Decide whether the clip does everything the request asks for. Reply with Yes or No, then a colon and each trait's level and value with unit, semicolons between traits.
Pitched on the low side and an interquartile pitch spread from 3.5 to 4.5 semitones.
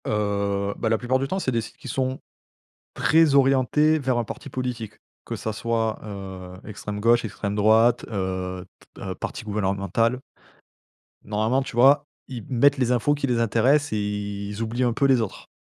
Yes: low, 115 Hz; average, 4.1 semitones